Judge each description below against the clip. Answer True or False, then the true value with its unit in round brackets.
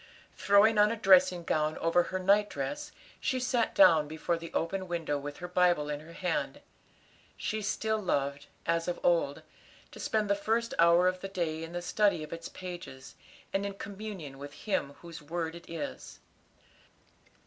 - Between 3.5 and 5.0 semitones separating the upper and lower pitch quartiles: True (4.0 semitones)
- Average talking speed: True (175 wpm)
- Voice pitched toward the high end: False (175 Hz)